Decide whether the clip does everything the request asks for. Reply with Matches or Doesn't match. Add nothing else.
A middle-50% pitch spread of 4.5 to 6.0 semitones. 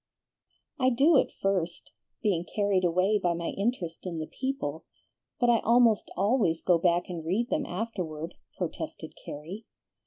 Matches